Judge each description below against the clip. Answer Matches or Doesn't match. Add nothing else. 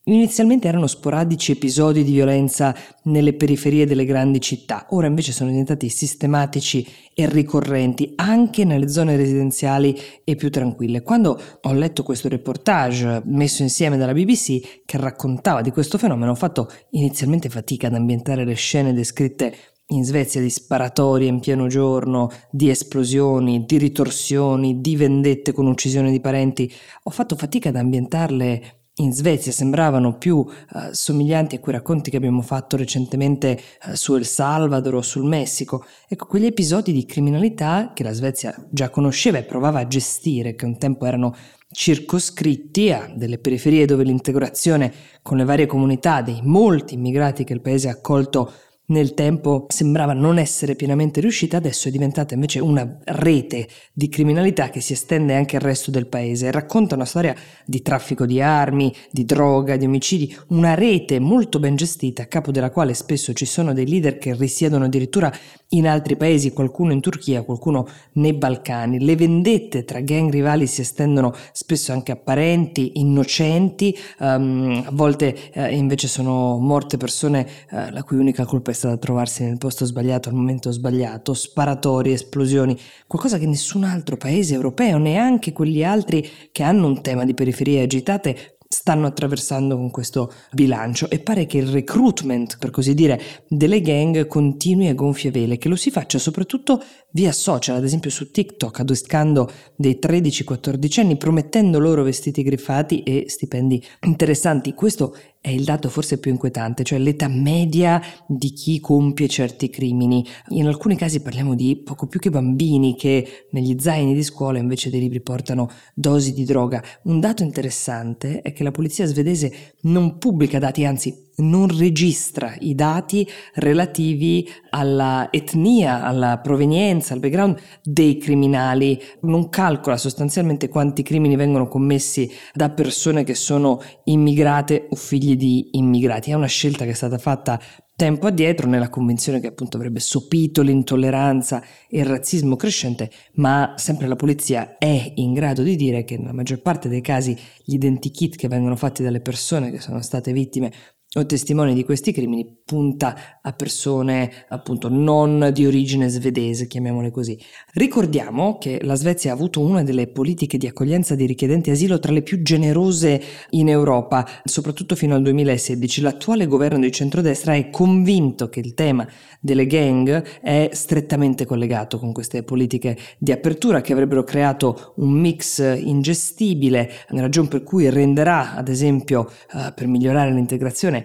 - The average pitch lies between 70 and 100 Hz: Doesn't match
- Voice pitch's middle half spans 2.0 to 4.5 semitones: Matches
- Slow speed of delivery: Doesn't match